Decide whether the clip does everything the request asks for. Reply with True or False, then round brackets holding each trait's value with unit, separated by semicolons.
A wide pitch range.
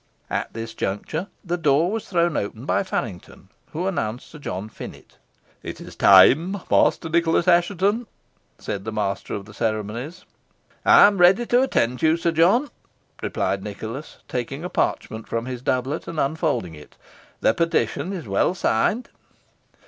True (8.0 semitones)